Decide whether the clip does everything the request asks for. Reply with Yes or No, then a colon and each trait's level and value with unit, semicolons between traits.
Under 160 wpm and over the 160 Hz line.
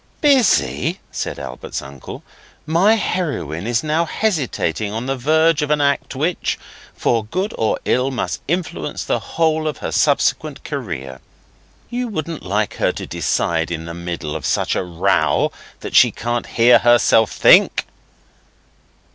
No: average, 140 wpm; low, 125 Hz